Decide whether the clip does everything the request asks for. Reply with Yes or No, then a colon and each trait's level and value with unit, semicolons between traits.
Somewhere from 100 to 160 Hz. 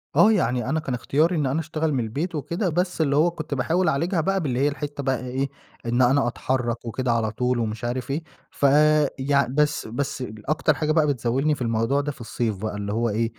Yes: low, 135 Hz